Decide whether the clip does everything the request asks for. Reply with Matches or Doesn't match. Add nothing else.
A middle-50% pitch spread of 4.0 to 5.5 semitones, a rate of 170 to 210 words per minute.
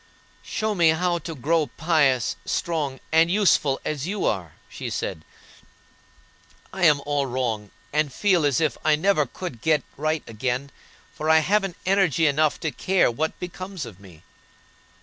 Doesn't match